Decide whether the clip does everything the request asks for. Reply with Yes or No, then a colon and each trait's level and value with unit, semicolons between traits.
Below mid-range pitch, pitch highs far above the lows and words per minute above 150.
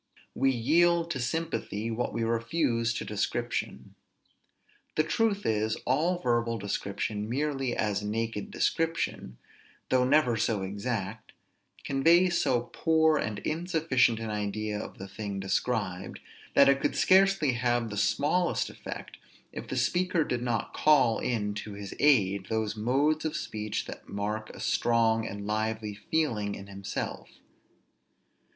No: low, 115 Hz; wide, 6.2 semitones; slow, 135 wpm